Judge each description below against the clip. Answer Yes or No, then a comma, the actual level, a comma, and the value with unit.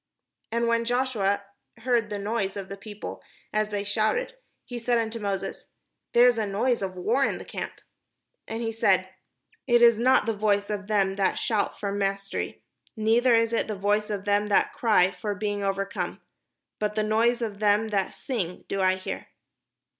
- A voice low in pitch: No, high, 210 Hz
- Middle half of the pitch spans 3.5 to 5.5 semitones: No, narrow, 2.5 semitones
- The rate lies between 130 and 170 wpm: No, average, 185 wpm